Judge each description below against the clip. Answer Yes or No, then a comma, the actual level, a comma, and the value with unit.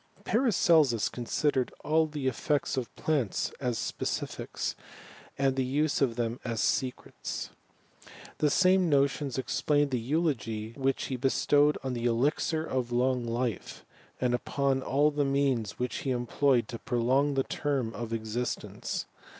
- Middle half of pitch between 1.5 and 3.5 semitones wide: Yes, average, 3.2 semitones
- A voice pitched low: Yes, low, 130 Hz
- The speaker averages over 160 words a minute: No, slow, 135 wpm